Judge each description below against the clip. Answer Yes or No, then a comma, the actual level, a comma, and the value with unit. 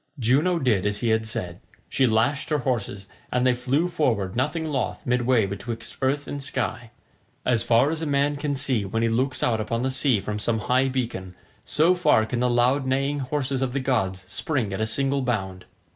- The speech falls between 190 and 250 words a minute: Yes, fast, 205 wpm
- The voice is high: No, low, 125 Hz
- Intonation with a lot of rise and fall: No, average, 3.8 semitones